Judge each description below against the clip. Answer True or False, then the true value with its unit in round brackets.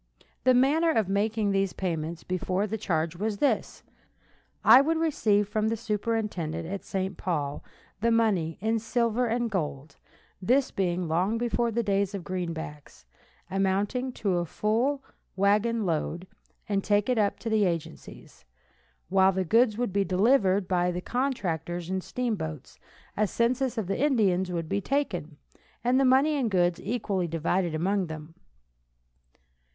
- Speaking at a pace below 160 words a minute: True (150 wpm)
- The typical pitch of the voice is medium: False (200 Hz)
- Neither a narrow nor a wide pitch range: True (4.6 semitones)